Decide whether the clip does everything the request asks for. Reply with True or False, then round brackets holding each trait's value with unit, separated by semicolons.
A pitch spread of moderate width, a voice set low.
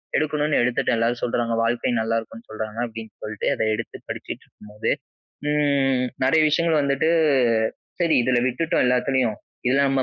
True (3.9 semitones; 125 Hz)